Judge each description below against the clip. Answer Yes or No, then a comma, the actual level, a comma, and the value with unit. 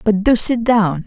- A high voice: Yes, high, 210 Hz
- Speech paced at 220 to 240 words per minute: Yes, fast, 225 wpm